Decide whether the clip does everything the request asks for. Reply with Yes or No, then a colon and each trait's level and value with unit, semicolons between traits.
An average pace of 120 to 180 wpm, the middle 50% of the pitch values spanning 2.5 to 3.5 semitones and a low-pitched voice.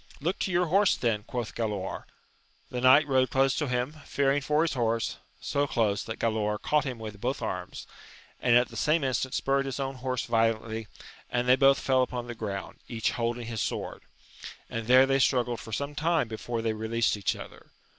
No: average, 195 wpm; average, 3.2 semitones; low, 125 Hz